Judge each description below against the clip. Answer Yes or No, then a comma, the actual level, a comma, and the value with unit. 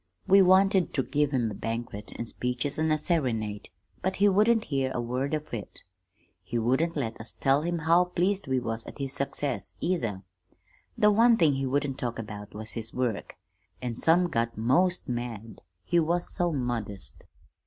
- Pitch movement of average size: No, wide, 6.9 semitones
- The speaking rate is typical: Yes, average, 180 wpm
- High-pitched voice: No, low, 135 Hz